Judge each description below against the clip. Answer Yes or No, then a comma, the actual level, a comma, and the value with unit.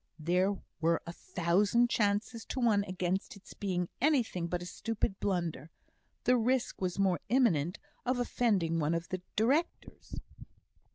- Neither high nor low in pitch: No, high, 195 Hz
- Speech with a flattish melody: No, average, 4.9 semitones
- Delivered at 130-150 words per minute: Yes, average, 145 wpm